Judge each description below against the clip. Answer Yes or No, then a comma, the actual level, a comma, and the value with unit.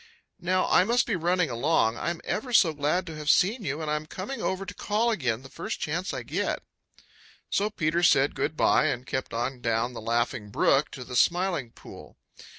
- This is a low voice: No, medium, 155 Hz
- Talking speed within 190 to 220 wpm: Yes, average, 200 wpm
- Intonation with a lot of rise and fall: Yes, wide, 6.4 semitones